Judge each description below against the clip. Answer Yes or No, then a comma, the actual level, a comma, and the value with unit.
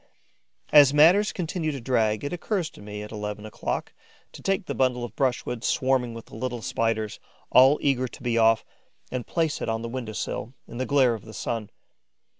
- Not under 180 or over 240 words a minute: Yes, average, 200 wpm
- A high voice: No, low, 125 Hz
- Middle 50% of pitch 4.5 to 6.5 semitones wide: No, average, 4.0 semitones